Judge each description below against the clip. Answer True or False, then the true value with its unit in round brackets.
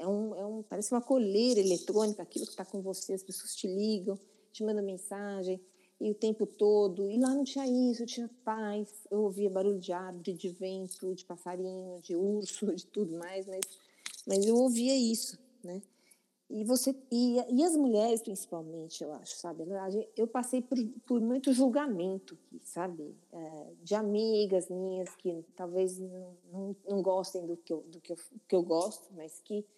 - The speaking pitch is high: True (200 Hz)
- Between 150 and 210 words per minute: True (160 wpm)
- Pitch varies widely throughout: False (3.0 semitones)